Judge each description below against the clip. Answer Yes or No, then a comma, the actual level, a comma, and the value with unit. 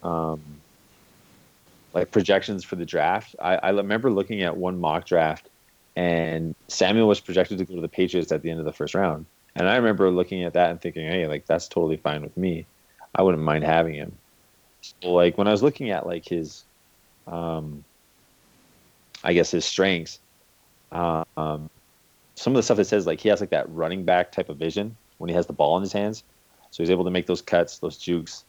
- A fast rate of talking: Yes, fast, 210 wpm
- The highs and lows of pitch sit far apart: No, average, 2.9 semitones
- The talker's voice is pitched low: Yes, very low, 90 Hz